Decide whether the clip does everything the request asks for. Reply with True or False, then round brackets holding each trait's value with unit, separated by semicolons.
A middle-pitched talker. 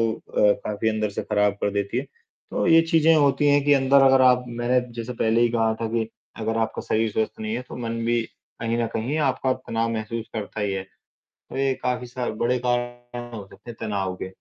False (120 Hz)